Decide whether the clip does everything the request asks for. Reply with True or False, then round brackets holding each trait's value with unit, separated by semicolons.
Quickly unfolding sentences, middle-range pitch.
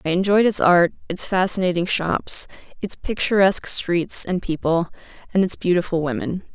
False (145 wpm; 180 Hz)